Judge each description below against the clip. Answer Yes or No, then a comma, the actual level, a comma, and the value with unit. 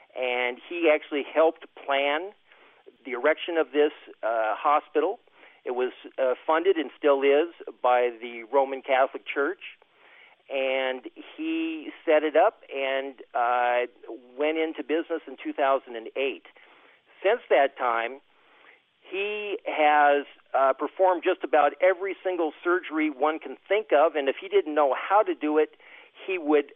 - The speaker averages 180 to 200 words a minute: No, average, 140 wpm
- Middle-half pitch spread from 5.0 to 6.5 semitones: Yes, wide, 5.4 semitones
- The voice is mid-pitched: Yes, medium, 150 Hz